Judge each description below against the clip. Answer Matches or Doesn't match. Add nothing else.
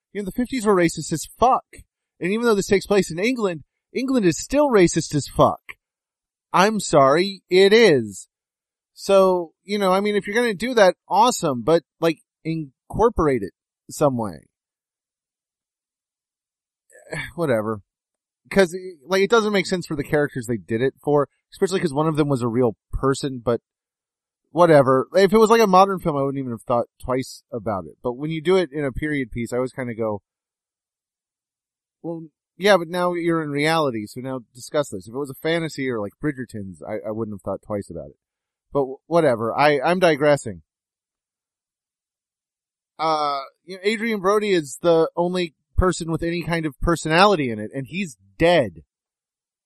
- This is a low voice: Doesn't match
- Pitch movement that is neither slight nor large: Doesn't match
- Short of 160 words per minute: Doesn't match